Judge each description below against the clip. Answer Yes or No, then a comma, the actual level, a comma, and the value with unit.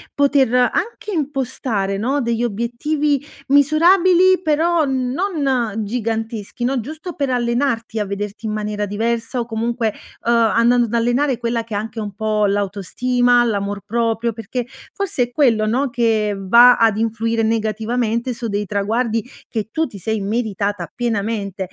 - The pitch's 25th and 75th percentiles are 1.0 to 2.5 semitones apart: No, average, 2.9 semitones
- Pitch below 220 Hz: No, high, 230 Hz